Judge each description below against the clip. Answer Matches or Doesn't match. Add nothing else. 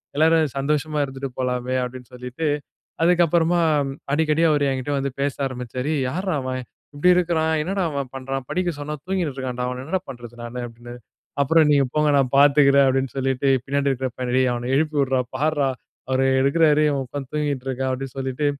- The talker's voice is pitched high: Doesn't match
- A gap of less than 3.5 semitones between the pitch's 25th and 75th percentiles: Matches